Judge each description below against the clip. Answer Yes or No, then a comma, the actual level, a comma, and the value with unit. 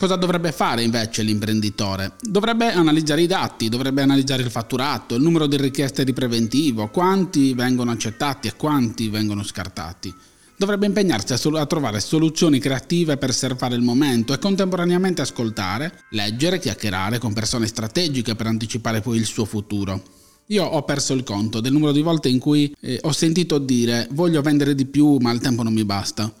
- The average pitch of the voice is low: Yes, low, 130 Hz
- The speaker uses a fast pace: Yes, fast, 175 wpm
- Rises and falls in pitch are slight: No, wide, 5.5 semitones